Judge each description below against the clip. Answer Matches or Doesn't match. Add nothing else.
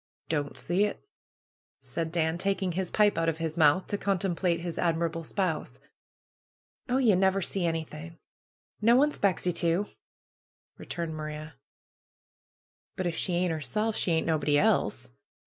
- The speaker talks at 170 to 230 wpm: Doesn't match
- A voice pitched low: Doesn't match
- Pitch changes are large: Doesn't match